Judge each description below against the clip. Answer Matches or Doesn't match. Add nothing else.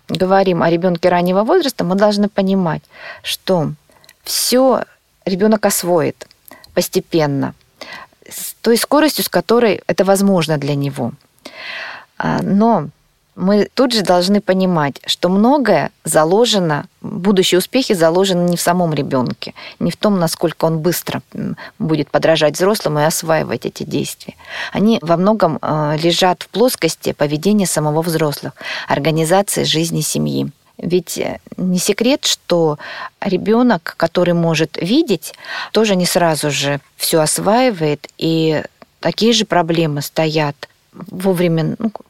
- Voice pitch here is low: Doesn't match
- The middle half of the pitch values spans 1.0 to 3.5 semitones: Doesn't match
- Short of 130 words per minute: Matches